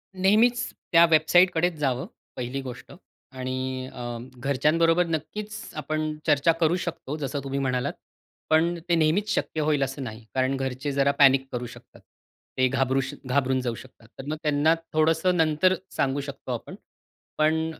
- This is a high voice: No, medium, 145 Hz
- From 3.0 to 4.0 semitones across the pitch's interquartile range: Yes, average, 3.7 semitones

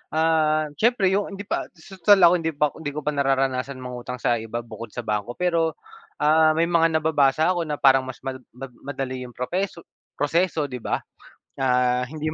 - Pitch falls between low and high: Yes, medium, 150 Hz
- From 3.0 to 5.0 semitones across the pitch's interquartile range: Yes, average, 4.3 semitones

